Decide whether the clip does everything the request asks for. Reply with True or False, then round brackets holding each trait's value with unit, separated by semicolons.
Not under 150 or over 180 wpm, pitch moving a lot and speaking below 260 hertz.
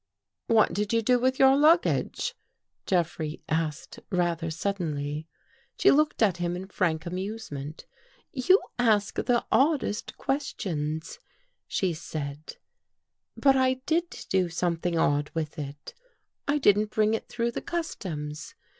False (140 wpm; 7.4 semitones; 185 Hz)